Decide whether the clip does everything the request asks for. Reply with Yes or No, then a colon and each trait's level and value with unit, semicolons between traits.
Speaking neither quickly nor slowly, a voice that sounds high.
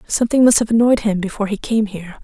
No: fast, 240 wpm; high, 215 Hz